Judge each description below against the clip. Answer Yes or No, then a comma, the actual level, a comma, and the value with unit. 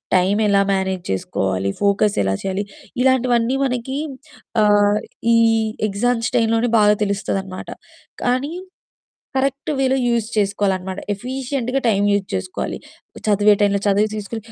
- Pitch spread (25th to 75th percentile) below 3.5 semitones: No, average, 3.8 semitones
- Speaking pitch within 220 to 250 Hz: No, high, 210 Hz